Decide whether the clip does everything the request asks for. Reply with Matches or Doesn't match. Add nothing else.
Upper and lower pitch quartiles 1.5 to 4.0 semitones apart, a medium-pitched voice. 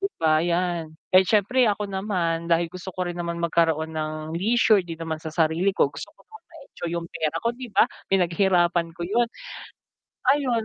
Matches